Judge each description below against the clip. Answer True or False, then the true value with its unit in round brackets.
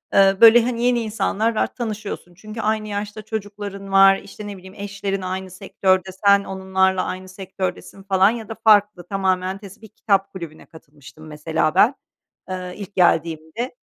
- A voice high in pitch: True (195 Hz)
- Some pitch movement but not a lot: False (2.2 semitones)